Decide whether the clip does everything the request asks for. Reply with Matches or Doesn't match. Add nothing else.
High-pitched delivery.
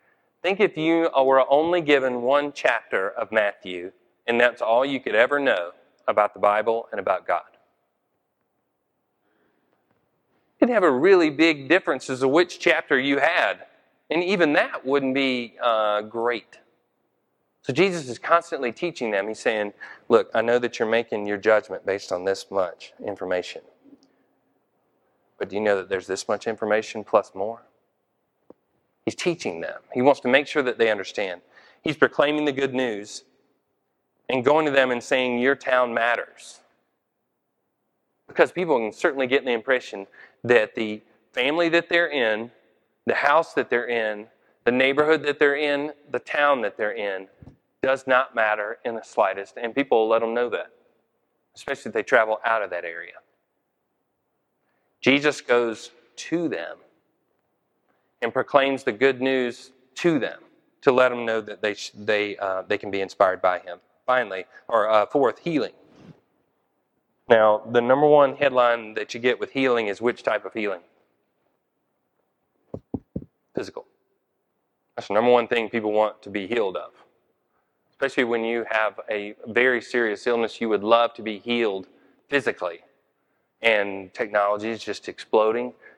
Doesn't match